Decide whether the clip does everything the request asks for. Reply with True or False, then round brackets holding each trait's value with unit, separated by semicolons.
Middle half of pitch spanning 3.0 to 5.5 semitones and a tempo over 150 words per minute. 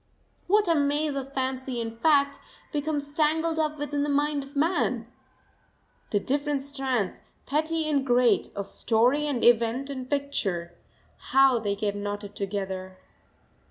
False (4.5 semitones; 140 wpm)